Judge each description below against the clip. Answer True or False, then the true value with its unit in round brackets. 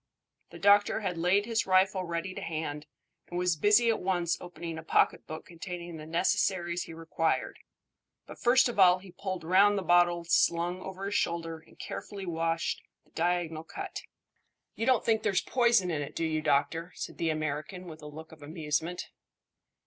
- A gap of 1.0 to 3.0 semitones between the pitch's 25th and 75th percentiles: True (2.7 semitones)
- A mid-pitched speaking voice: True (175 Hz)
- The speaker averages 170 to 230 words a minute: True (180 wpm)